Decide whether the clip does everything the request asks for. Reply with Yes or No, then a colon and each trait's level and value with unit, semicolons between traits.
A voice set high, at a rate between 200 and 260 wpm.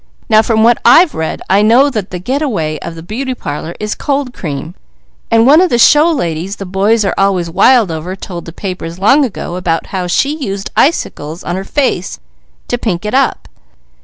Yes: high, 200 Hz; fast, 205 wpm